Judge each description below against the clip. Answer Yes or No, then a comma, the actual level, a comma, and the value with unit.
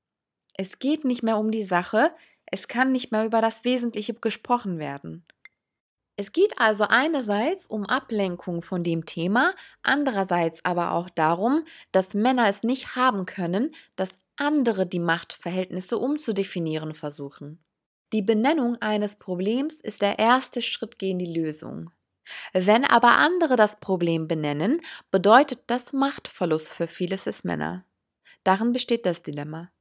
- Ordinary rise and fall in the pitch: No, wide, 6.2 semitones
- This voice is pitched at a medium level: No, high, 210 Hz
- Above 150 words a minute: No, average, 140 wpm